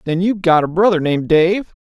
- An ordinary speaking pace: No, fast, 230 wpm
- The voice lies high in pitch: No, medium, 175 Hz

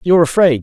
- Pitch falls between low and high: Yes, medium, 160 Hz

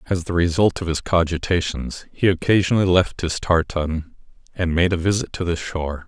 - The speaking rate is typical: Yes, average, 180 wpm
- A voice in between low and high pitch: No, very low, 85 Hz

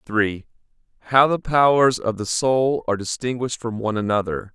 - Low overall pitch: Yes, low, 120 Hz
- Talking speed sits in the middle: Yes, average, 160 wpm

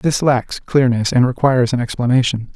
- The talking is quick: No, average, 165 wpm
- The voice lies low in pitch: Yes, low, 125 Hz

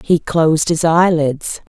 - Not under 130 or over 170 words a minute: Yes, slow, 135 wpm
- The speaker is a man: No, female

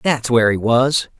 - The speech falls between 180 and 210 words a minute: Yes, average, 200 wpm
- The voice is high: No, low, 125 Hz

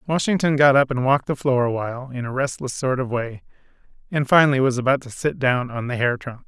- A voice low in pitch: Yes, low, 130 Hz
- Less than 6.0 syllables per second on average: No, 6.1 syllables/s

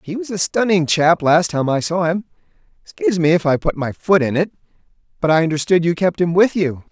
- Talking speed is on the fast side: Yes, fast, 225 wpm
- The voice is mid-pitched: Yes, medium, 165 Hz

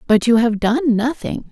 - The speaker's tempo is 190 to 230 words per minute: Yes, average, 200 wpm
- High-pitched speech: Yes, high, 240 Hz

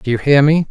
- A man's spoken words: Yes, male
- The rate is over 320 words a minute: Yes, fast, 340 wpm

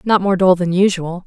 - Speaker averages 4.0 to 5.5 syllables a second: Yes, 5.1 syllables/s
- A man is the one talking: No, female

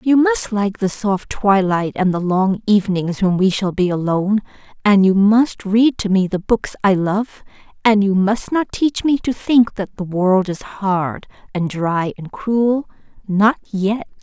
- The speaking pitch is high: Yes, high, 205 Hz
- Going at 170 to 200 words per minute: Yes, average, 180 wpm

